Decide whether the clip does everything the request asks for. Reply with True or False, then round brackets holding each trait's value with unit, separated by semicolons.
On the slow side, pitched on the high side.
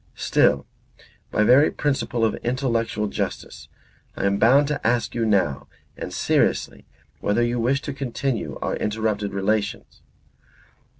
False (130 wpm; 115 Hz)